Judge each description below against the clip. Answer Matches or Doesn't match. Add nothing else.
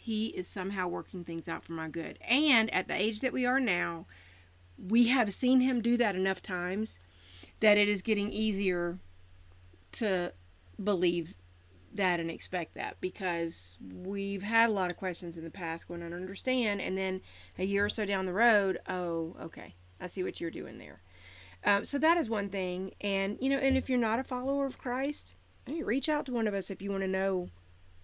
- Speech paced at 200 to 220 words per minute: Matches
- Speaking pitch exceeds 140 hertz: Matches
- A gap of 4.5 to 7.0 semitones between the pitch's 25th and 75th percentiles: Matches